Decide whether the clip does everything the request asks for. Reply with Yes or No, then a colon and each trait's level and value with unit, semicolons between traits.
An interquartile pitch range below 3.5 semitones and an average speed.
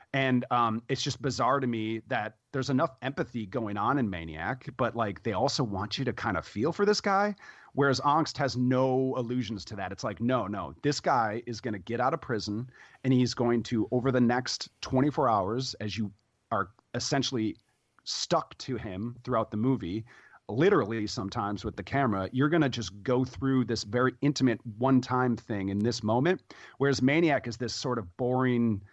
Yes: average, 3.1 semitones; average, 195 wpm